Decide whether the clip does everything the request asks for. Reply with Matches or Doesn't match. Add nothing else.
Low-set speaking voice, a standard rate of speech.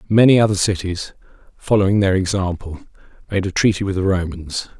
Matches